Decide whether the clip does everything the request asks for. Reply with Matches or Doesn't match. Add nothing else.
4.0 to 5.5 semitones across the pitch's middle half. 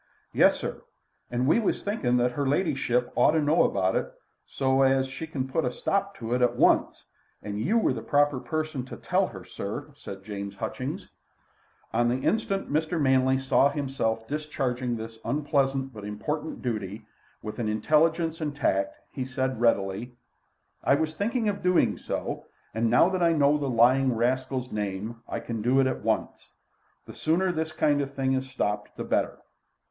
Matches